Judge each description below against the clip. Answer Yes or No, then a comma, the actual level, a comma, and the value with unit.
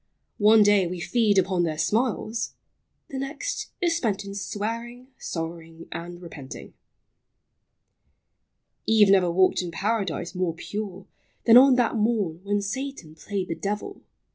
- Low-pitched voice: No, high, 200 Hz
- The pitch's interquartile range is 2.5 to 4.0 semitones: No, average, 4.5 semitones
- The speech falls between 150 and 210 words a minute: No, average, 140 wpm